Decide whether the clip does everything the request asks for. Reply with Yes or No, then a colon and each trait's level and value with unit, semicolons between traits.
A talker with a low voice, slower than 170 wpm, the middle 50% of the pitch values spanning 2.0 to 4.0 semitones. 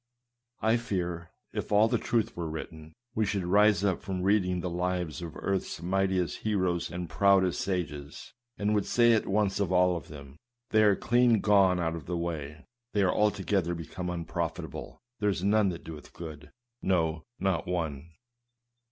No: very low, 90 Hz; average, 175 wpm; average, 3.4 semitones